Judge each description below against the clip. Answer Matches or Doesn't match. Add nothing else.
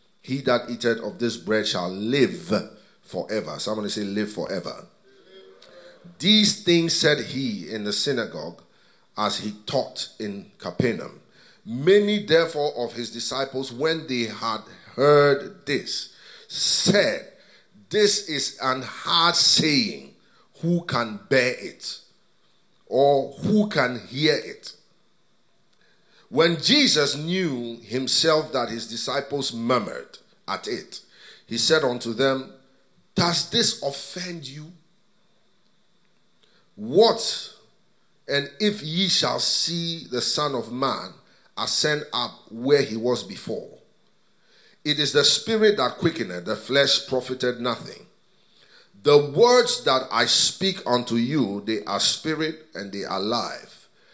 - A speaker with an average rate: Doesn't match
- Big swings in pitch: Matches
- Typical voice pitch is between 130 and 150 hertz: Matches